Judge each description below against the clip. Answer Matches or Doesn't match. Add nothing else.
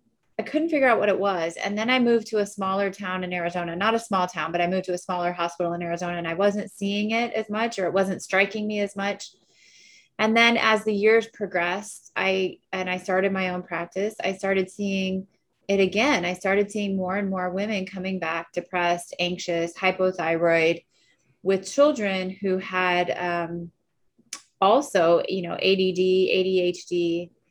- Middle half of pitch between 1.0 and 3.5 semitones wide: Matches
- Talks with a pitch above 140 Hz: Matches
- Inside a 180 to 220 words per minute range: Matches